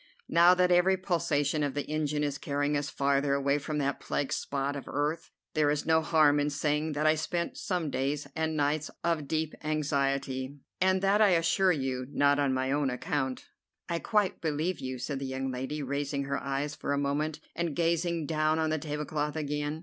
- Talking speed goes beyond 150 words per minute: Yes, average, 195 wpm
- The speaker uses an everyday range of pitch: No, narrow, 2.2 semitones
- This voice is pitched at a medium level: Yes, medium, 150 Hz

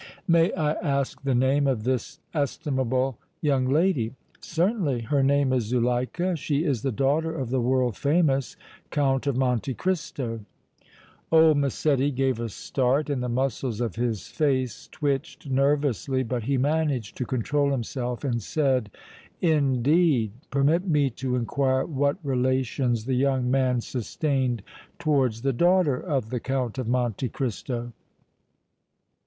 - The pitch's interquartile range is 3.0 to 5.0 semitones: No, narrow, 2.6 semitones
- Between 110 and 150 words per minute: Yes, average, 140 wpm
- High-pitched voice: No, low, 135 Hz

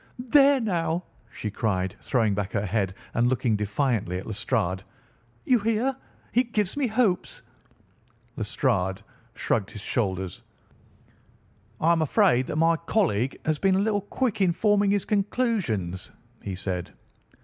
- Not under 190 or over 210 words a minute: No, average, 140 wpm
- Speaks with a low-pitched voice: No, medium, 150 Hz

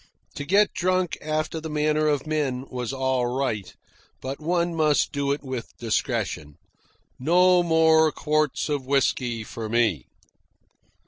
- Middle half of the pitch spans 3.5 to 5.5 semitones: Yes, average, 3.9 semitones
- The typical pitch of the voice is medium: Yes, medium, 145 Hz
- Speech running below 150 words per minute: Yes, slow, 135 wpm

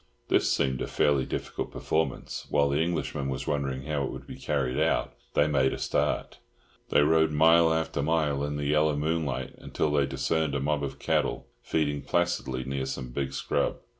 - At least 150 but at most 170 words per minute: No, average, 185 wpm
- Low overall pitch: Yes, very low, 75 Hz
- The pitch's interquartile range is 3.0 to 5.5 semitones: No, narrow, 2.5 semitones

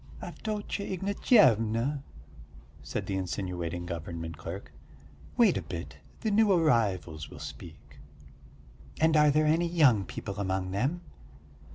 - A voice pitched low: Yes, low, 110 Hz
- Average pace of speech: No, slow, 120 wpm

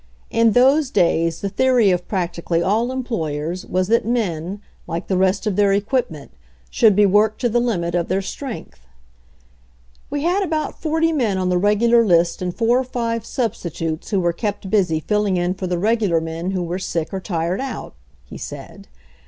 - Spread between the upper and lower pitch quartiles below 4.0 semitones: No, average, 5.1 semitones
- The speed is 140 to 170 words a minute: No, average, 185 wpm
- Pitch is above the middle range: Yes, high, 195 Hz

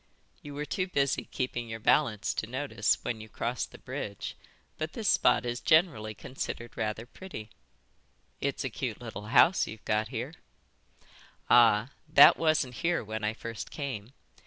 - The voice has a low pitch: Yes, low, 120 Hz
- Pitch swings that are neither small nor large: Yes, average, 4.9 semitones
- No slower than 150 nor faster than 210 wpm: Yes, average, 160 wpm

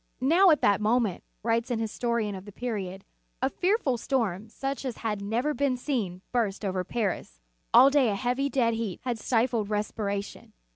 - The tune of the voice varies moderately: Yes, average, 4.0 semitones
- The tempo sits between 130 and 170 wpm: No, average, 185 wpm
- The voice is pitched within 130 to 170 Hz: No, high, 230 Hz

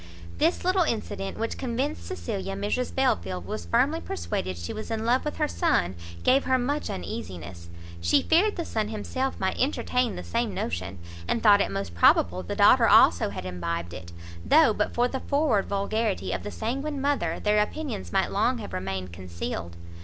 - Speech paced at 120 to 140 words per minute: No, average, 180 wpm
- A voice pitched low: No, high, 200 Hz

